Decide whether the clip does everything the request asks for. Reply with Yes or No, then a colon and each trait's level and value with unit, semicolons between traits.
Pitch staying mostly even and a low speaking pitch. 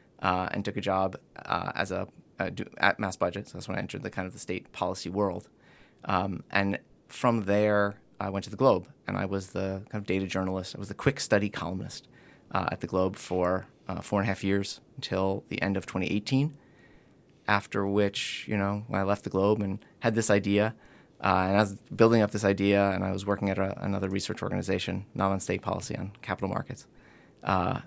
Yes: narrow, 1.6 semitones; low, 100 Hz